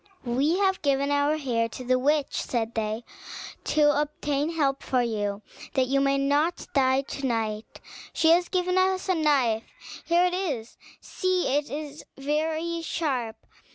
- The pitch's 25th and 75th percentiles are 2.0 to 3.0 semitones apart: No, average, 4.2 semitones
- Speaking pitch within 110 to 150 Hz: No, very high, 285 Hz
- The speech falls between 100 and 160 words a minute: Yes, average, 155 wpm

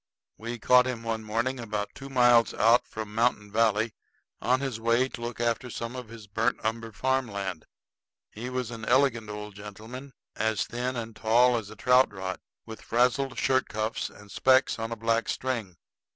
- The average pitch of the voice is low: Yes, low, 115 Hz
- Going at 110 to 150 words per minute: No, average, 180 wpm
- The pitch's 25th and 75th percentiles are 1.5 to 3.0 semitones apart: Yes, narrow, 2.5 semitones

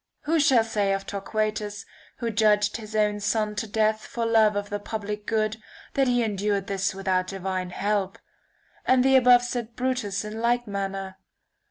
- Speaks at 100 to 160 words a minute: No, average, 170 wpm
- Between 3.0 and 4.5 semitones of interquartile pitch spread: No, narrow, 2.4 semitones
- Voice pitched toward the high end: Yes, high, 210 Hz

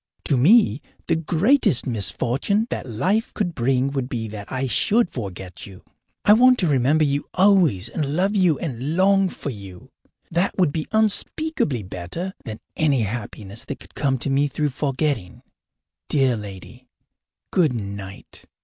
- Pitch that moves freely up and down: Yes, wide, 7.8 semitones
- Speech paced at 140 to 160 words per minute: Yes, average, 155 wpm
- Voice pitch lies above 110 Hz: Yes, medium, 140 Hz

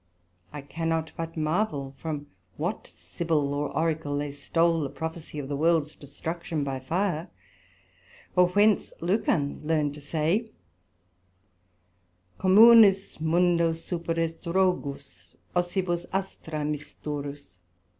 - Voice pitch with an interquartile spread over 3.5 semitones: No, average, 3.2 semitones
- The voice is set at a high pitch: No, medium, 160 Hz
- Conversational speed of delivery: No, slow, 105 wpm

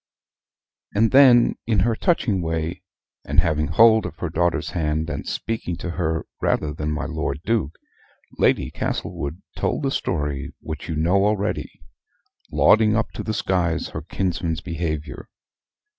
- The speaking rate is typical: Yes, average, 145 wpm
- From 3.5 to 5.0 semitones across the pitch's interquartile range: No, wide, 5.5 semitones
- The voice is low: Yes, very low, 85 Hz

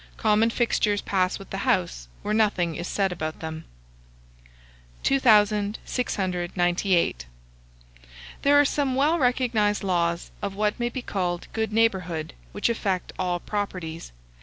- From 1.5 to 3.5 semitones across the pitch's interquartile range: No, average, 4.3 semitones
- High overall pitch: Yes, high, 200 Hz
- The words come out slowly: Yes, slow, 125 wpm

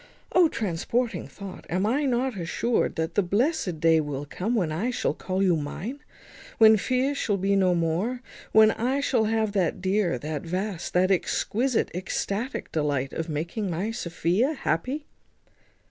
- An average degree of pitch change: No, wide, 5.9 semitones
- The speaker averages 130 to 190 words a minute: Yes, average, 160 wpm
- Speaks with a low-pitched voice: No, high, 195 Hz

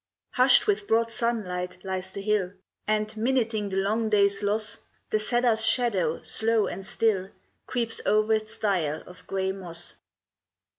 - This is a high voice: Yes, high, 210 Hz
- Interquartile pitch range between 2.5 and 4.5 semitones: Yes, average, 2.8 semitones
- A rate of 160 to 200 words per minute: No, average, 145 wpm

